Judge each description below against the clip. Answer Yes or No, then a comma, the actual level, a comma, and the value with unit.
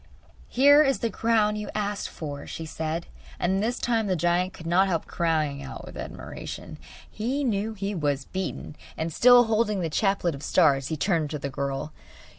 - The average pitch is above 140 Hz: Yes, medium, 185 Hz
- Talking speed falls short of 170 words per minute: No, average, 185 wpm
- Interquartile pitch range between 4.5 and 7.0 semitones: Yes, wide, 5.6 semitones